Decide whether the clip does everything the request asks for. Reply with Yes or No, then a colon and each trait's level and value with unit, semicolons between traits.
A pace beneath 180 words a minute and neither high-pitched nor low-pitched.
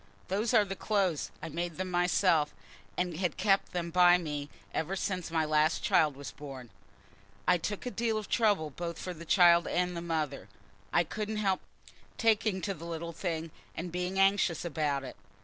No: average, 185 wpm; medium, 175 Hz